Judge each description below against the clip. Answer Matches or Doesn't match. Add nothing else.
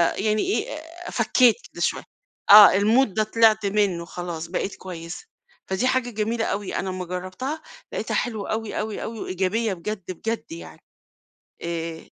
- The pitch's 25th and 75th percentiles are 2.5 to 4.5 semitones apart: Matches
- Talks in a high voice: Matches